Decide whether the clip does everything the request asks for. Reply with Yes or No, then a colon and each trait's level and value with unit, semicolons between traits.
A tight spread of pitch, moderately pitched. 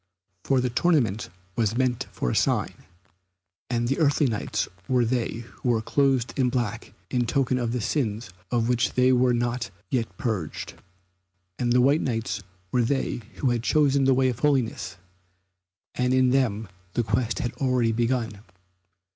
No: narrow, 2.1 semitones; low, 125 Hz